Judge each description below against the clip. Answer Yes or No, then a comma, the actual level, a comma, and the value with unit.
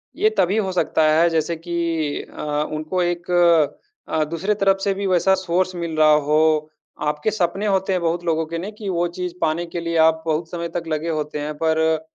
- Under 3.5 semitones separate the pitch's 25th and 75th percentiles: Yes, narrow, 2.6 semitones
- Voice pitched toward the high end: No, medium, 170 Hz